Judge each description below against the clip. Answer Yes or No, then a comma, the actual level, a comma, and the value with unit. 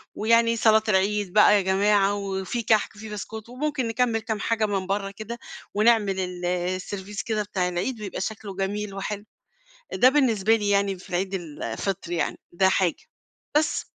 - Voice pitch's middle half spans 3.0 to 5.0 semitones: No, narrow, 2.5 semitones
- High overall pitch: Yes, high, 205 Hz